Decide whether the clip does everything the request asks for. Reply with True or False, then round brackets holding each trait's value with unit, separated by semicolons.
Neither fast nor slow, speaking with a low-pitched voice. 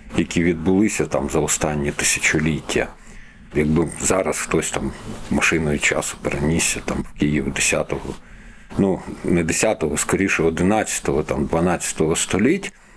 True (115 wpm; 80 Hz)